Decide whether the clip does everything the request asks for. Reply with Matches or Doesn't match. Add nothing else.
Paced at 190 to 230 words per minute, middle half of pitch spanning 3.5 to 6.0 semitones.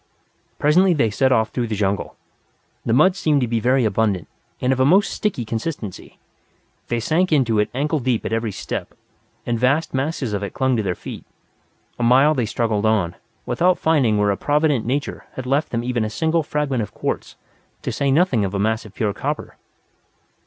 Matches